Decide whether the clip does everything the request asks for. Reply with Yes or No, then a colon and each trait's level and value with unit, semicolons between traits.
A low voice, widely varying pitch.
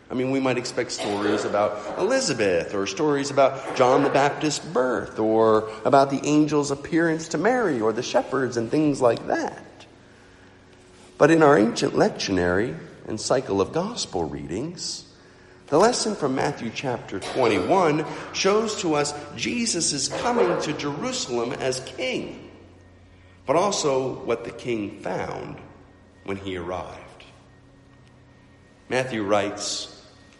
Yes: low, 125 Hz; wide, 6.4 semitones